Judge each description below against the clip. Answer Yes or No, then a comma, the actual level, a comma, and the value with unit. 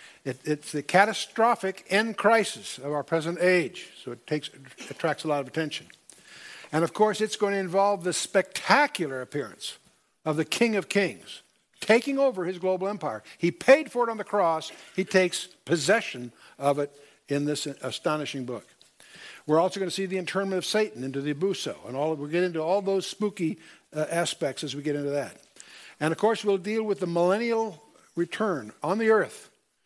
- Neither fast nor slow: Yes, average, 190 wpm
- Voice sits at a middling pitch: Yes, medium, 180 Hz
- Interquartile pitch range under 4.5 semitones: No, average, 5.2 semitones